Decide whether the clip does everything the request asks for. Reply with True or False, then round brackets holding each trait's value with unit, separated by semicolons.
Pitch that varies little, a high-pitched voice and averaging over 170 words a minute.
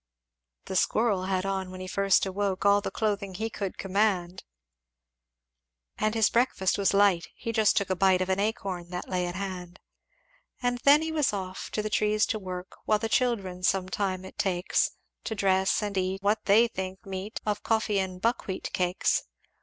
True (2.3 semitones; 195 Hz; 190 wpm)